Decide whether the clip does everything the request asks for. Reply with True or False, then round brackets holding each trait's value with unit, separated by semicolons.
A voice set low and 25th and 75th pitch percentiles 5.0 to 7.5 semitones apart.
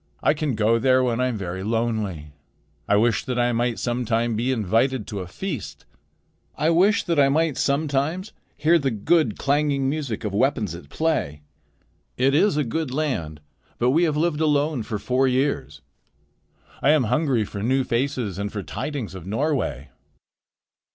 True (125 Hz; 5.6 semitones)